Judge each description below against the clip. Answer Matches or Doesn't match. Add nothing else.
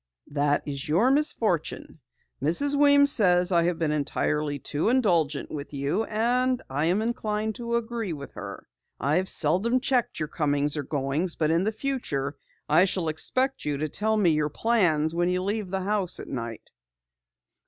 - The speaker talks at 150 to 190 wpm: Matches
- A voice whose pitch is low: Doesn't match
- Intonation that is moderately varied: Doesn't match